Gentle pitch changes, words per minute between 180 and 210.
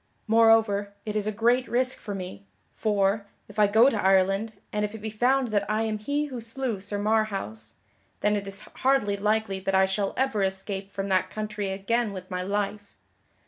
Yes: narrow, 2.2 semitones; average, 195 wpm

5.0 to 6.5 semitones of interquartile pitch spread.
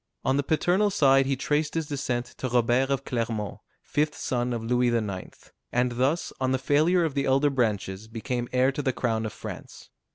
No: average, 3.0 semitones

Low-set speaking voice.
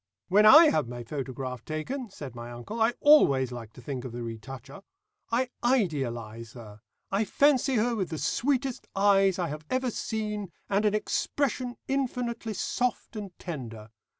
No: high, 195 Hz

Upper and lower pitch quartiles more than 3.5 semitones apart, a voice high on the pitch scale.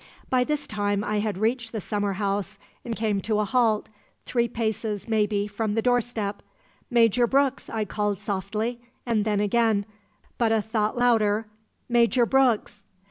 No: narrow, 2.4 semitones; high, 220 Hz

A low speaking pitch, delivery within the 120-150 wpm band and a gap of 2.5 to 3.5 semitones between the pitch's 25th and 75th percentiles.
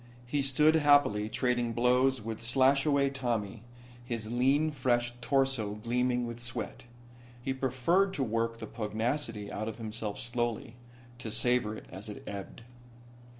Yes: low, 120 Hz; average, 140 wpm; average, 2.9 semitones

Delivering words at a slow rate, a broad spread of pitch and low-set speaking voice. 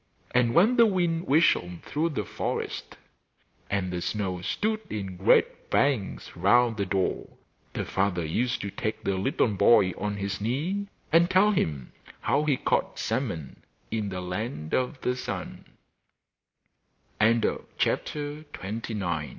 Yes: slow, 125 wpm; wide, 7.7 semitones; low, 110 Hz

